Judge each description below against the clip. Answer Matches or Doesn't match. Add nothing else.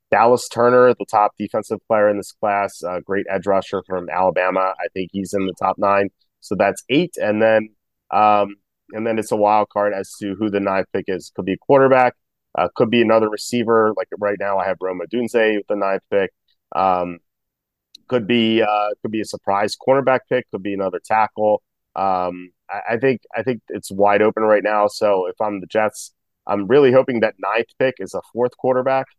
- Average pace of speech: Doesn't match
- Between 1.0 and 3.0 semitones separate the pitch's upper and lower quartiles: Matches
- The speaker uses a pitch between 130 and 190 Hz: Doesn't match